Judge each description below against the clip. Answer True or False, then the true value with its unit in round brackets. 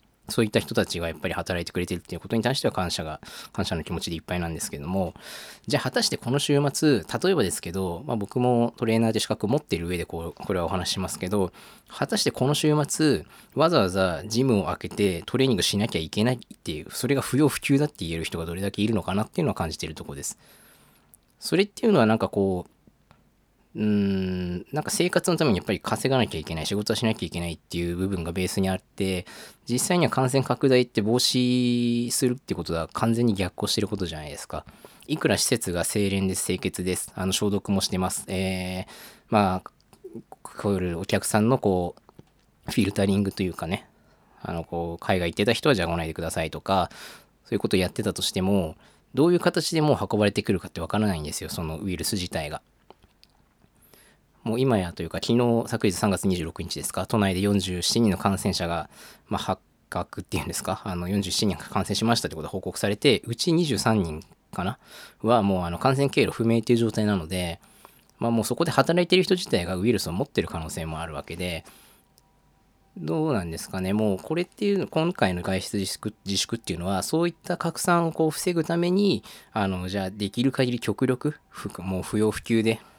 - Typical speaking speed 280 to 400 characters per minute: False (425 characters per minute)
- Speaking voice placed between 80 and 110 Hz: True (100 Hz)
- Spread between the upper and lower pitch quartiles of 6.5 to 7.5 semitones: False (5.2 semitones)